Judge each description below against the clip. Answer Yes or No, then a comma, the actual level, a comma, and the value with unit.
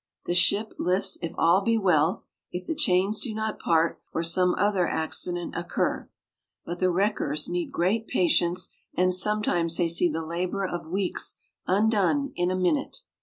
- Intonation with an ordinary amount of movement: Yes, average, 3.0 semitones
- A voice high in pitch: No, medium, 180 Hz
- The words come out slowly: No, average, 165 wpm